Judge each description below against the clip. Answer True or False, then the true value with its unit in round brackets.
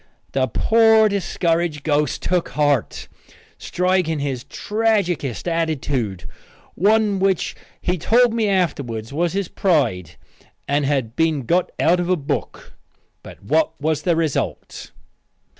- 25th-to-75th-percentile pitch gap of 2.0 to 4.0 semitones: False (4.8 semitones)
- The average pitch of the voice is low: False (165 Hz)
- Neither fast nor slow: False (125 wpm)